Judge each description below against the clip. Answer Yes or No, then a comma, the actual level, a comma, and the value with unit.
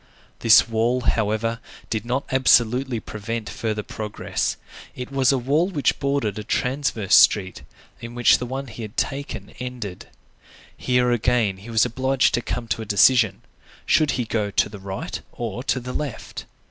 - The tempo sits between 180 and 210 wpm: No, average, 165 wpm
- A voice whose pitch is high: No, low, 120 Hz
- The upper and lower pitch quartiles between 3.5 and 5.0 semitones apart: No, average, 3.0 semitones